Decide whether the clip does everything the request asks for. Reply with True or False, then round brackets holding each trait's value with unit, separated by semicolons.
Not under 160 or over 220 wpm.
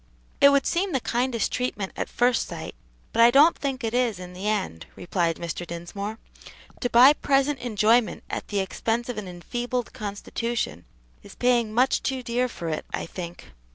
True (180 wpm)